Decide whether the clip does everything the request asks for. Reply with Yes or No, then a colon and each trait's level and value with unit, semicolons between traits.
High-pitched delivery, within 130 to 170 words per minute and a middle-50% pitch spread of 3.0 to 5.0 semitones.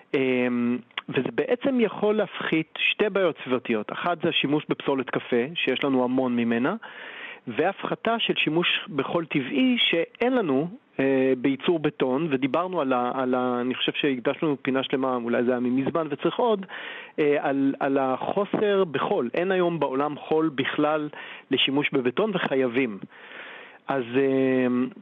No: medium, 140 Hz; average, 135 wpm; average, 4.7 semitones